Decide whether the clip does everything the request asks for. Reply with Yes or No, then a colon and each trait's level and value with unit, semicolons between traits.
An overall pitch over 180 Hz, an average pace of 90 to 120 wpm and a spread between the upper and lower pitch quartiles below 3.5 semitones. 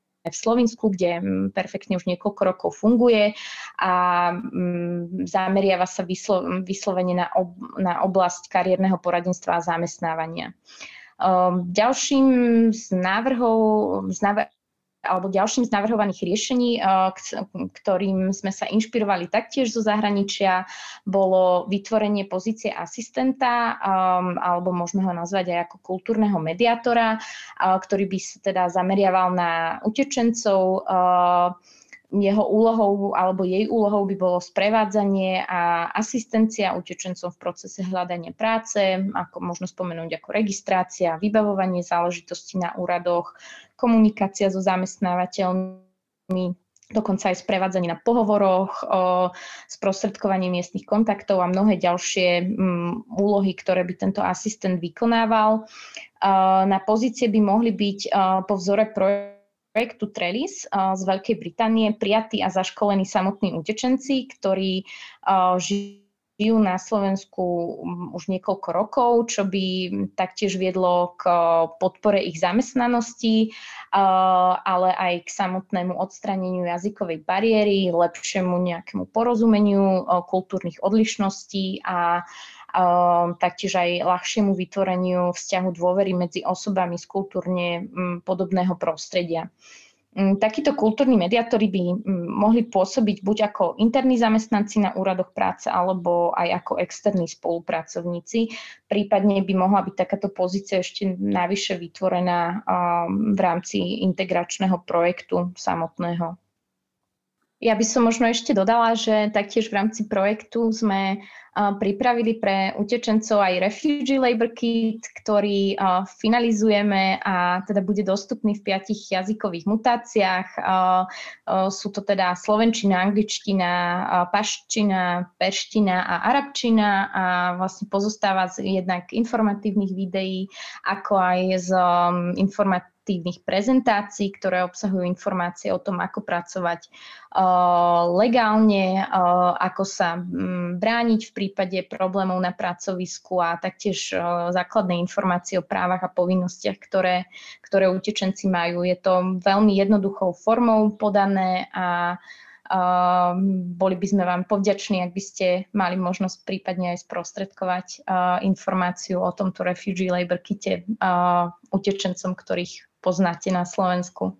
Yes: high, 190 Hz; slow, 110 wpm; narrow, 2.6 semitones